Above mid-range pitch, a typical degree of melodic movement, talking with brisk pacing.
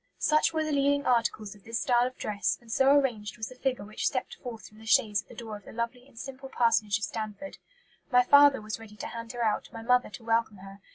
Yes: high, 230 Hz; average, 3.2 semitones; fast, 250 wpm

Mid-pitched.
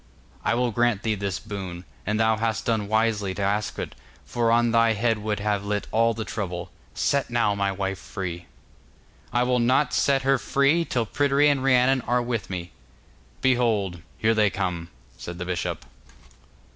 No: low, 110 Hz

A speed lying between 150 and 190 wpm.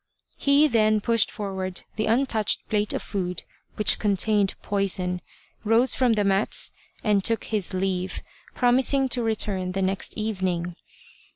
No: slow, 135 wpm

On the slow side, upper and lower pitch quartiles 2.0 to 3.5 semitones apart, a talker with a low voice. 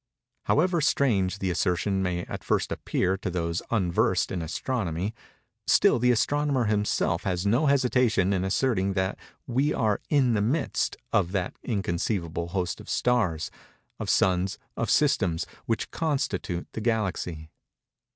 No: slow, 130 wpm; wide, 5.5 semitones; low, 100 Hz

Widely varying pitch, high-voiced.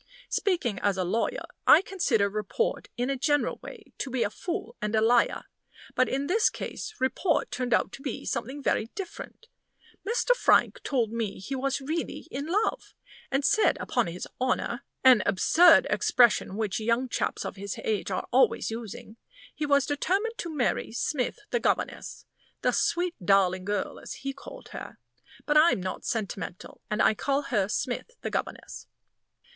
Yes: wide, 6.2 semitones; very high, 255 Hz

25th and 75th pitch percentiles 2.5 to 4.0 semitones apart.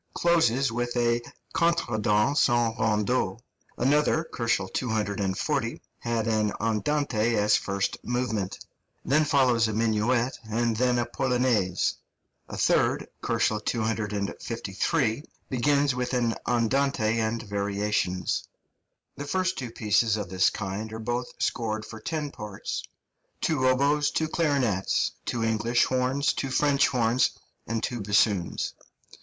Yes: average, 3.4 semitones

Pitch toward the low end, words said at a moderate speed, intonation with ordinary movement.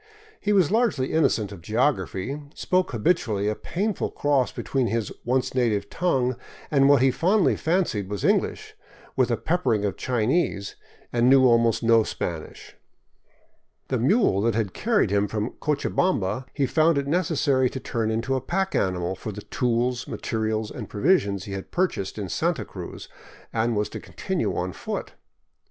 No: low, 120 Hz; average, 160 wpm; wide, 6.0 semitones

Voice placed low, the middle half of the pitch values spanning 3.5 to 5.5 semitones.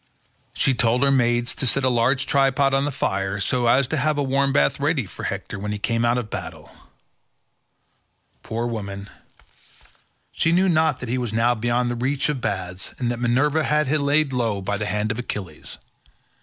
Yes: low, 120 Hz; average, 4.3 semitones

